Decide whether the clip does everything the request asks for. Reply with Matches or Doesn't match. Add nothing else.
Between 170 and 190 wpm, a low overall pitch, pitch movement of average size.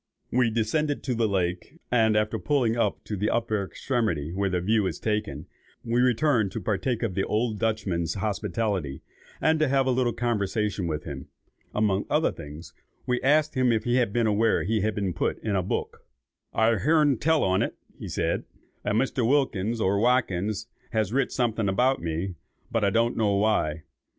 Matches